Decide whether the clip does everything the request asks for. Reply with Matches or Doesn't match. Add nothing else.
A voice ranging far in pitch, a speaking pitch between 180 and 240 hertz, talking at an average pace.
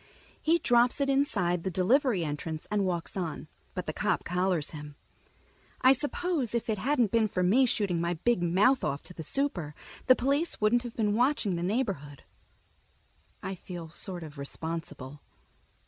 Matches